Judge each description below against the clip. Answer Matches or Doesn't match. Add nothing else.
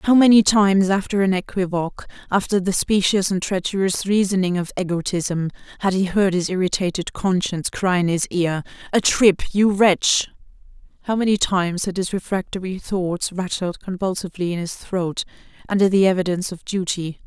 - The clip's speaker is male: Doesn't match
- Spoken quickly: Doesn't match